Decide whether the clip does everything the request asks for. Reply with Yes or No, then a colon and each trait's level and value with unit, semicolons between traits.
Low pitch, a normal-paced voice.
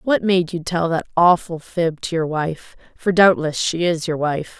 No: medium, 170 Hz; average, 195 wpm